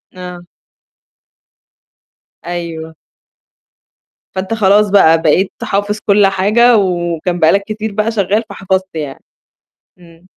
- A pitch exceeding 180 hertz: Yes, high, 190 Hz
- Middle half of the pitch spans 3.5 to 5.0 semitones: No, average, 3.1 semitones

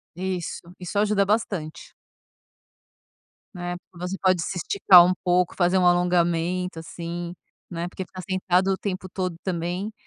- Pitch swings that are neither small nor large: No, narrow, 1.3 semitones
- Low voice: No, medium, 180 Hz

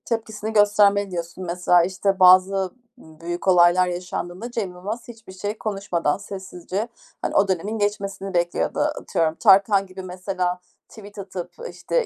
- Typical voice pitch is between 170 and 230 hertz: Yes, high, 190 Hz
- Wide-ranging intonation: No, narrow, 2.4 semitones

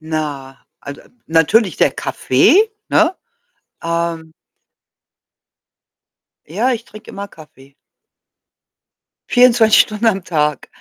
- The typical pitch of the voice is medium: Yes, medium, 170 Hz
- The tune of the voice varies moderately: No, wide, 6.6 semitones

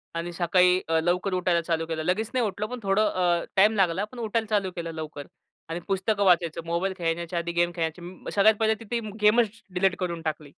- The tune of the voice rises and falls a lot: No, average, 3.5 semitones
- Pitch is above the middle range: No, medium, 180 Hz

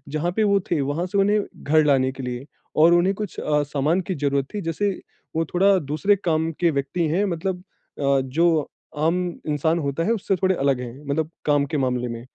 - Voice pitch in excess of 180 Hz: No, medium, 160 Hz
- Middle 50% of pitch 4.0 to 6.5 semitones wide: Yes, average, 4.3 semitones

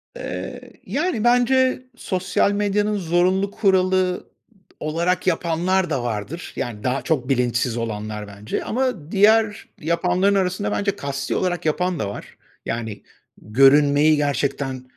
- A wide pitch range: Yes, wide, 6.7 semitones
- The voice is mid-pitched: Yes, medium, 170 Hz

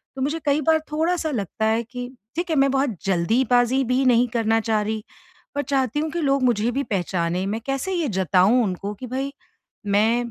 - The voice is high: Yes, high, 245 Hz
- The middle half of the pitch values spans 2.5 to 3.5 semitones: No, average, 4.4 semitones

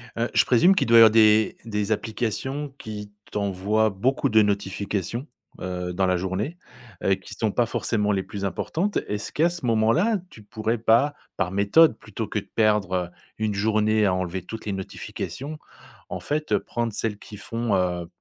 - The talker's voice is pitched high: No, low, 110 Hz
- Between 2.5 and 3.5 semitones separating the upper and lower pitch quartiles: Yes, average, 2.9 semitones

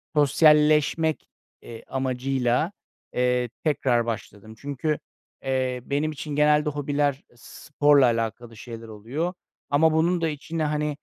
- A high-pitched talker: No, medium, 140 Hz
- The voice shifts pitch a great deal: No, average, 3.5 semitones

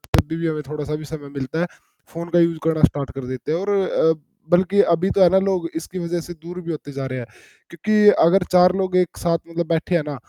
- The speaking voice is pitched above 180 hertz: No, medium, 170 Hz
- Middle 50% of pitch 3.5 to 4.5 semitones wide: No, average, 2.9 semitones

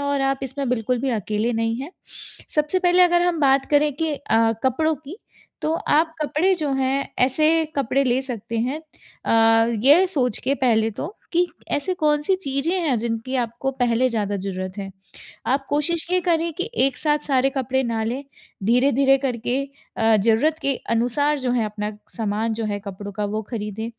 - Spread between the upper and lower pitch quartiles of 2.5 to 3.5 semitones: No, average, 4.8 semitones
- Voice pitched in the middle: No, very high, 265 Hz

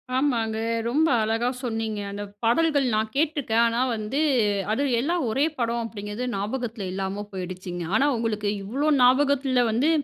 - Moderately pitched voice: No, high, 230 Hz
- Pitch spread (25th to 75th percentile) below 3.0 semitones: No, average, 4.0 semitones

